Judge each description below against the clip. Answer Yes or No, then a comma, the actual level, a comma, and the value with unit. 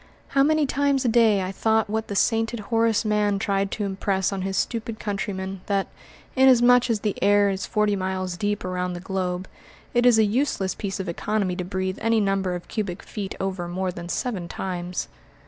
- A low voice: No, high, 200 Hz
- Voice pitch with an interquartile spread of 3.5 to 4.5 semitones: No, average, 2.8 semitones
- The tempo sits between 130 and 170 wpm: No, average, 195 wpm